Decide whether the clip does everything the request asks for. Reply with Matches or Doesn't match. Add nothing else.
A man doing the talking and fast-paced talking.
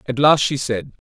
Matches